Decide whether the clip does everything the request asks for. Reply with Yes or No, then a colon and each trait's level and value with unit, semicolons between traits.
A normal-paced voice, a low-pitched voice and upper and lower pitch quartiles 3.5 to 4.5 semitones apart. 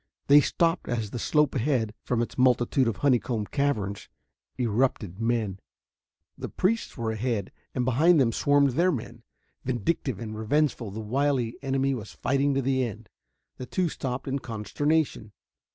Yes: average, 150 wpm; low, 125 Hz; average, 4.0 semitones